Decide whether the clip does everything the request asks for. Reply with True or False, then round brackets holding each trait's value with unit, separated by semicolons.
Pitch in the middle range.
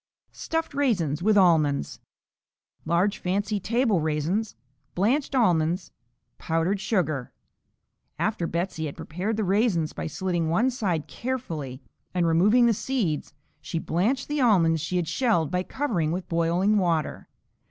True (180 Hz)